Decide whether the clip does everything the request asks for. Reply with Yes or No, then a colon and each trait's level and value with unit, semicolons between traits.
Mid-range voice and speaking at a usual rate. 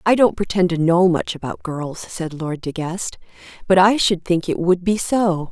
No: medium, 180 Hz; fast, 220 wpm